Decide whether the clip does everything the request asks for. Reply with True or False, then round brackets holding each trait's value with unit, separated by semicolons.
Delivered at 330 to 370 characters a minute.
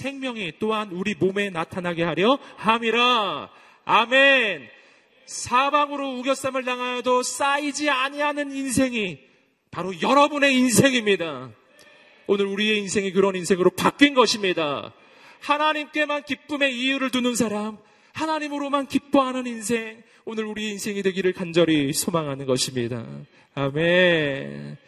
False (300 characters per minute)